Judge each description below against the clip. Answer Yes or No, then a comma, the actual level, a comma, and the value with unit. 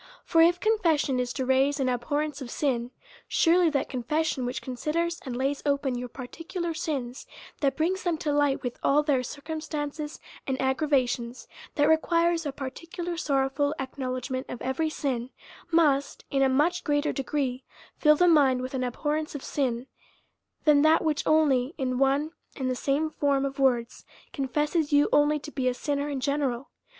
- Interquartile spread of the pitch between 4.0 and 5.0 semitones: No, average, 3.0 semitones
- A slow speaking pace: No, average, 180 wpm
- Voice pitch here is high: Yes, very high, 285 Hz